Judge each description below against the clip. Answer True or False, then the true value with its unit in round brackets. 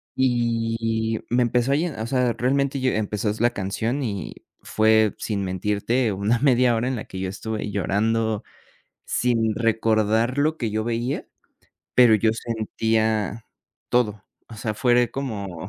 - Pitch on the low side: True (115 Hz)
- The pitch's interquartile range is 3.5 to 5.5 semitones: False (2.4 semitones)